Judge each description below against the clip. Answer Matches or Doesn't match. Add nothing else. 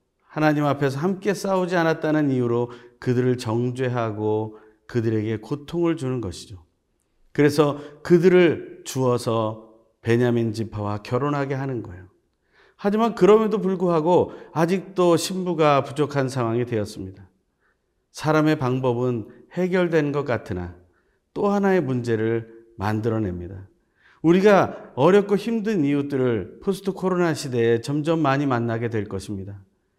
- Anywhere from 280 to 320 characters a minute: Matches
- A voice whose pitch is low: Matches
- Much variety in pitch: Matches